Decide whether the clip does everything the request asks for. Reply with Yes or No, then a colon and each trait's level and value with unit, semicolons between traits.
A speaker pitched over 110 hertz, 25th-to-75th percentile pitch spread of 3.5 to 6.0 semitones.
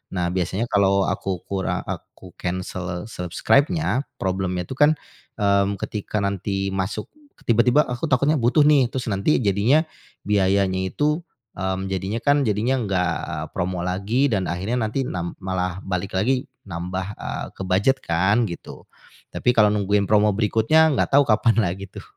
No: low, 100 Hz; average, 4.4 semitones